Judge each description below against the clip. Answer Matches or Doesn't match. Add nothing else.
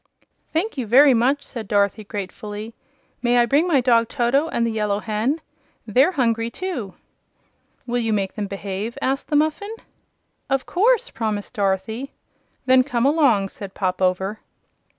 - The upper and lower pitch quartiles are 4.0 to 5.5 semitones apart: Matches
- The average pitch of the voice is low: Doesn't match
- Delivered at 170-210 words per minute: Doesn't match